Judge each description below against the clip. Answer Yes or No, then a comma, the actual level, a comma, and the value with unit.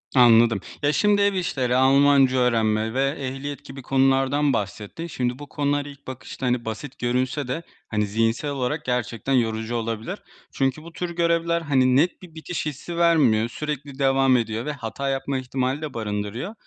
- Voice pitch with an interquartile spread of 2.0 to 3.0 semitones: No, average, 3.5 semitones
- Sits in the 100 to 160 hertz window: Yes, low, 135 Hz